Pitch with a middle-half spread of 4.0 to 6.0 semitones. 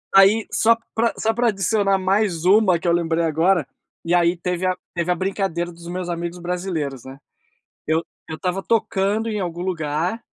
No: narrow, 2.6 semitones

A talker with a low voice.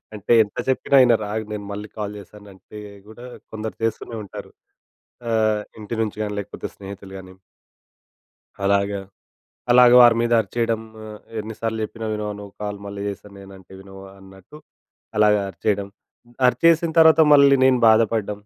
Yes: low, 105 Hz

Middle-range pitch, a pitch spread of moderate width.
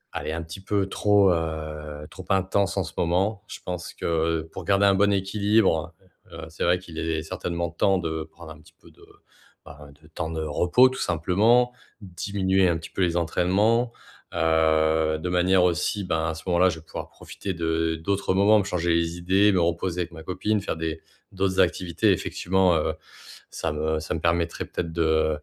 No: very low, 85 Hz; average, 3.0 semitones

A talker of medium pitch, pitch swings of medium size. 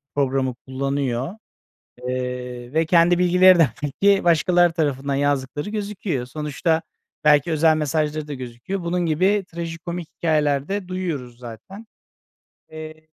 Yes: medium, 155 Hz; average, 4.3 semitones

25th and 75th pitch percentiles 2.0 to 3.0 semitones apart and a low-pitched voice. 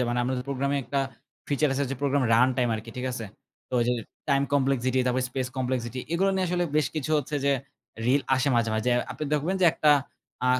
Yes: narrow, 2.4 semitones; low, 130 Hz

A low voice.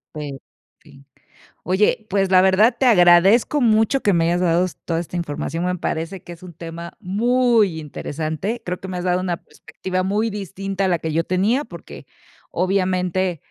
No: medium, 185 Hz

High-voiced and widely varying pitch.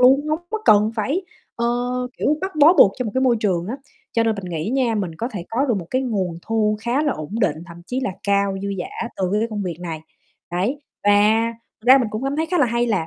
No: high, 225 Hz; average, 5.0 semitones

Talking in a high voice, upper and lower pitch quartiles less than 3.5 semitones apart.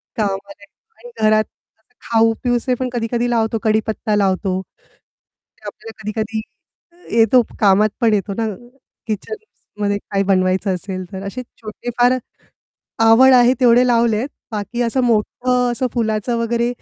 Yes: high, 225 Hz; average, 2.8 semitones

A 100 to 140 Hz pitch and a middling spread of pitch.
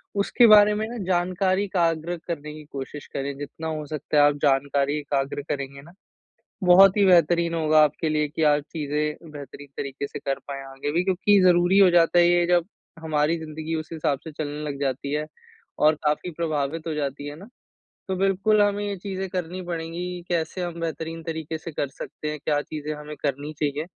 No: medium, 160 Hz; average, 3.2 semitones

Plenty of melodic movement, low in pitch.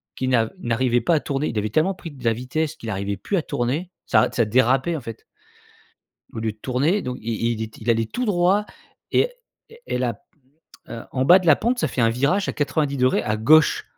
Yes: wide, 5.8 semitones; low, 130 Hz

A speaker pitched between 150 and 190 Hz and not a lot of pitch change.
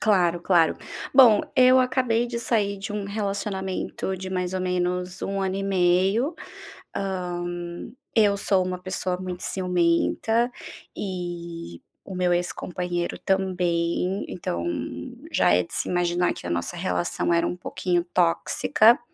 Yes: medium, 185 Hz; narrow, 2.2 semitones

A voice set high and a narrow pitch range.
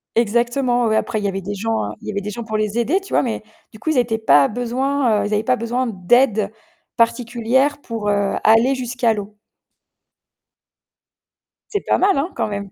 No: high, 230 Hz; average, 3.1 semitones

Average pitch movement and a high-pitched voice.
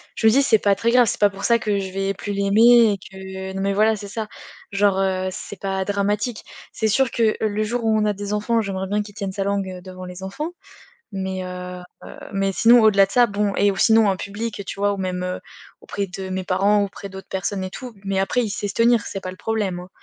No: narrow, 2.1 semitones; high, 200 Hz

